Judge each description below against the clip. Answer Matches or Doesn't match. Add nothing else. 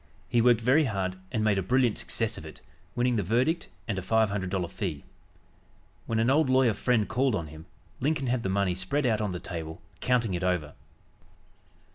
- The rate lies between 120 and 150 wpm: Doesn't match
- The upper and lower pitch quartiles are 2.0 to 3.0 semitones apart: Doesn't match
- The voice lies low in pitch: Matches